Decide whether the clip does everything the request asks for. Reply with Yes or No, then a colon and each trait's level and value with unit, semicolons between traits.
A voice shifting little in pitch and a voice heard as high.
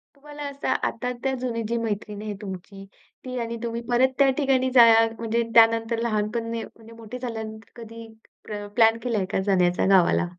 Yes: narrow, 2.2 semitones; high, 230 Hz